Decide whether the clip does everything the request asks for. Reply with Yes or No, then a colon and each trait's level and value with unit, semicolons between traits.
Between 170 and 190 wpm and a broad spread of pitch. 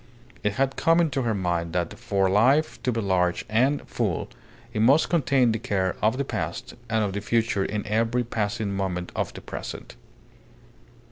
No: average, 180 wpm; average, 4.3 semitones